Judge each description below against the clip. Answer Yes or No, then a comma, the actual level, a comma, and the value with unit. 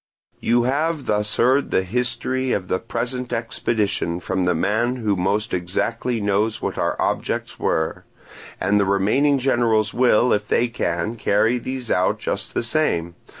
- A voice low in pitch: Yes, low, 115 Hz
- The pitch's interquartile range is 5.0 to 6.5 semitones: No, average, 3.9 semitones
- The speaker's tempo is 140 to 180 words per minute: Yes, average, 155 wpm